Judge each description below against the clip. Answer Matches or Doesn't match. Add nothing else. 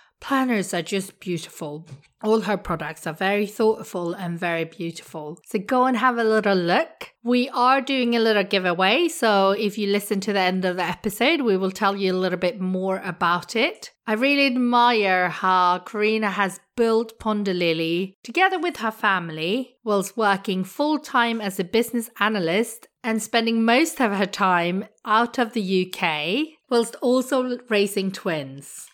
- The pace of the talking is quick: Doesn't match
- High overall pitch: Matches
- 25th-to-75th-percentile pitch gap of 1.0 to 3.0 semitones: Doesn't match